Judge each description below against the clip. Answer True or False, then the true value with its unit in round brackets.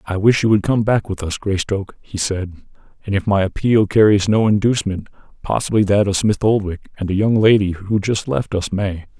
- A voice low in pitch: True (100 Hz)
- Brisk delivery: True (210 wpm)